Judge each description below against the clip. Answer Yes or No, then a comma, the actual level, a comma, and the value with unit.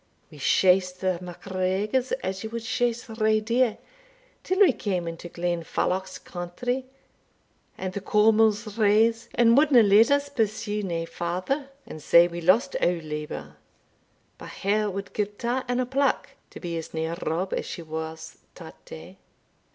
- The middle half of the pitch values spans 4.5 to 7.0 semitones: Yes, average, 4.9 semitones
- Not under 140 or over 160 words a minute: Yes, average, 155 wpm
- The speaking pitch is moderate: No, high, 200 Hz